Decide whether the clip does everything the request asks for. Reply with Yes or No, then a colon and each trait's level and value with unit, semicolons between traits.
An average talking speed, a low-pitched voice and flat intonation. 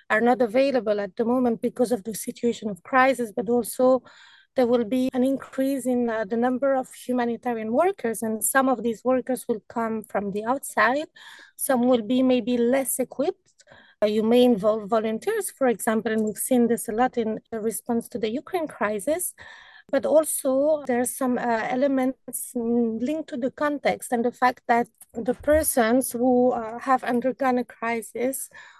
No: average, 175 wpm; high, 245 Hz; narrow, 2.3 semitones